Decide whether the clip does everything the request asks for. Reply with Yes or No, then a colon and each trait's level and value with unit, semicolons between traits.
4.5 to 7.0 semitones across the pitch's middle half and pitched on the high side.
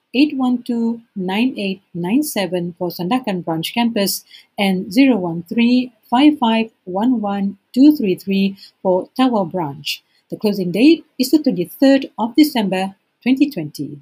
Yes: wide, 5.5 semitones; high, 210 Hz